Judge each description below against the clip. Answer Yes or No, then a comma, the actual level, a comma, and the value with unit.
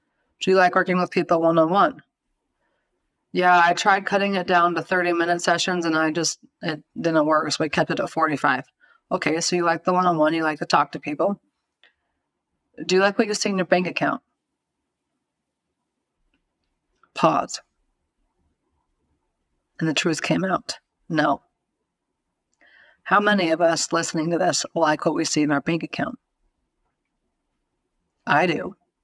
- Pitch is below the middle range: No, medium, 170 Hz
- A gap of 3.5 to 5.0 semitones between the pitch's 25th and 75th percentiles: No, narrow, 2.5 semitones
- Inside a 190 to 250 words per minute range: No, average, 165 wpm